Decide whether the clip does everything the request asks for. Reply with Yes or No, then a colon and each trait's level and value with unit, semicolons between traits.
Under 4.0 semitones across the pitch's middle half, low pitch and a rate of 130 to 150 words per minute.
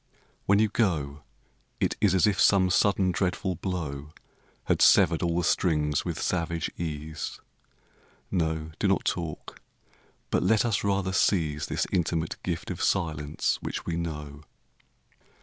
Yes: average, 3.4 semitones; very low, 85 Hz; average, 140 wpm